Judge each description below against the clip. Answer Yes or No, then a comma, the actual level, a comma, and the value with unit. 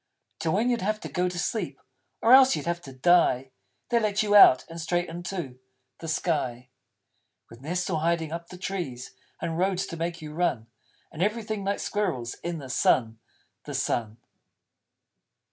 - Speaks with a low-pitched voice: No, medium, 170 Hz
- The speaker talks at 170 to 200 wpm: Yes, average, 175 wpm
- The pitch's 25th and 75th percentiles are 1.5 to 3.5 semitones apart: No, average, 5.1 semitones